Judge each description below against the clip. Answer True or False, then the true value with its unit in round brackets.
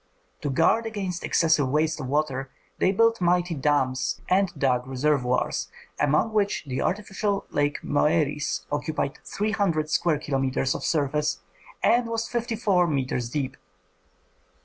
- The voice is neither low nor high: True (155 Hz)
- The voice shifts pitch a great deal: True (6.1 semitones)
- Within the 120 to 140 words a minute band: True (135 wpm)